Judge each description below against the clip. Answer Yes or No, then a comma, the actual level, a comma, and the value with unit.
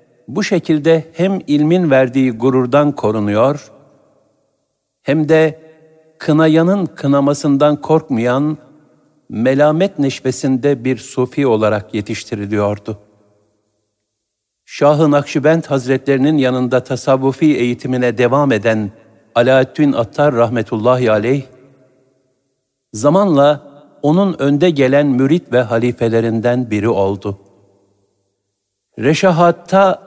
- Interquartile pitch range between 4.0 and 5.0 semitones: Yes, average, 4.7 semitones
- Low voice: Yes, low, 130 Hz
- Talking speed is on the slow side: Yes, slow, 80 wpm